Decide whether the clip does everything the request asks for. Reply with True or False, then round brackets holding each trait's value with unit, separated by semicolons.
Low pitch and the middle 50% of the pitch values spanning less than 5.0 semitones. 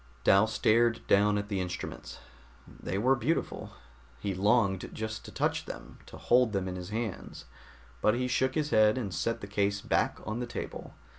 True (110 Hz; 3.1 semitones)